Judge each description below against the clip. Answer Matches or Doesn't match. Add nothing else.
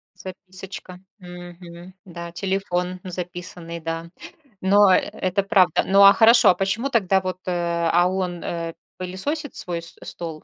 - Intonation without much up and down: Matches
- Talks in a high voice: Doesn't match